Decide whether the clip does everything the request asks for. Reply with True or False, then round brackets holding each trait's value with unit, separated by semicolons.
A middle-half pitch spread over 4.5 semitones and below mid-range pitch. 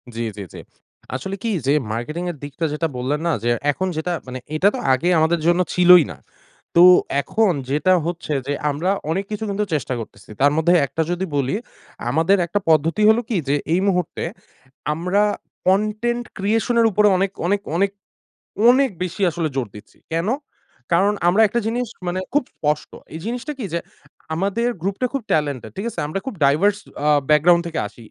False (5.1 semitones; 175 Hz)